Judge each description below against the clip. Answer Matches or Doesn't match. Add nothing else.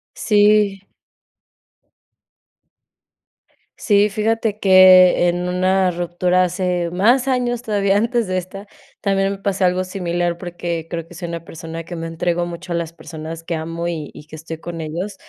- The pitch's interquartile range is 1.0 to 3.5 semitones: Matches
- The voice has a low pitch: Doesn't match